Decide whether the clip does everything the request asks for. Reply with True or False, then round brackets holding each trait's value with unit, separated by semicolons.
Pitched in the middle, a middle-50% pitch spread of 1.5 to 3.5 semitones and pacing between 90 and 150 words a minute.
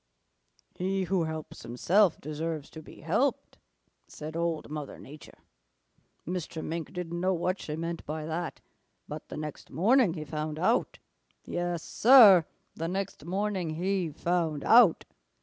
True (170 Hz; 2.9 semitones; 140 wpm)